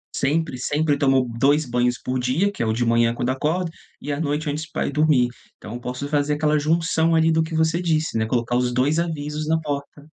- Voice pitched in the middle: Yes, medium, 145 Hz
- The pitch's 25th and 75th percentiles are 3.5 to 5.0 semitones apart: Yes, average, 3.9 semitones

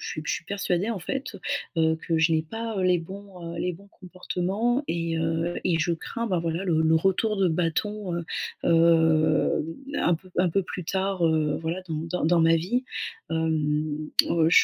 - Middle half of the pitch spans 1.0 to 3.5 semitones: Yes, average, 2.9 semitones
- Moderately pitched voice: Yes, medium, 170 Hz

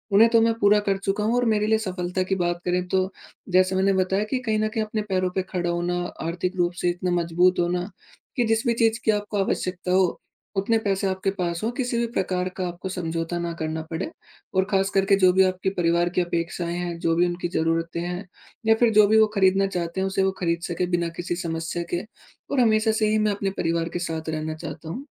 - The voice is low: No, medium, 185 Hz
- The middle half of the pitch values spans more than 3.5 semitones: No, average, 2.8 semitones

